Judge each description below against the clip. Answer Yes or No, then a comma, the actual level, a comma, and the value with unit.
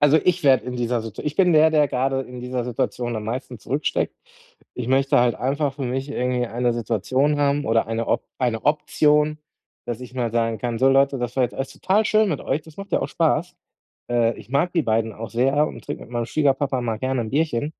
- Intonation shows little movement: No, average, 3.6 semitones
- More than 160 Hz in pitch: No, low, 130 Hz